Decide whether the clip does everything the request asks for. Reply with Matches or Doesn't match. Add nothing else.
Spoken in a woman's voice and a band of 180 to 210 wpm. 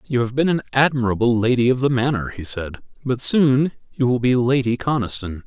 Doesn't match